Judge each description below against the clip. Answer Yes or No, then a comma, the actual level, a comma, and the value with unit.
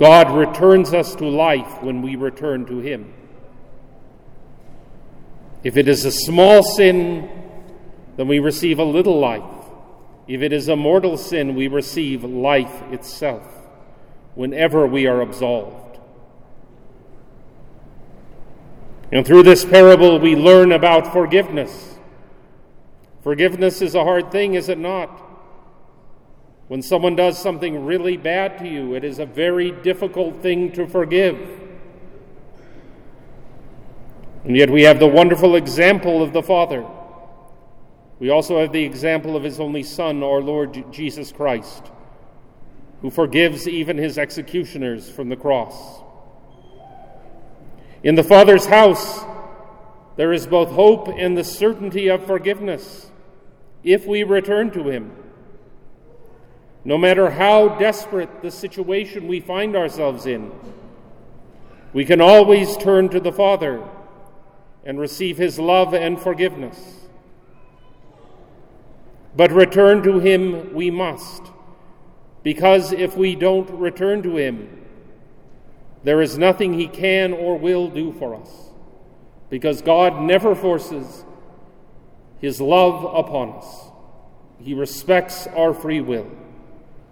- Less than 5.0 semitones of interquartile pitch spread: Yes, average, 4.4 semitones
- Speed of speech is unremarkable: No, slow, 120 wpm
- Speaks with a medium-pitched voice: Yes, medium, 175 Hz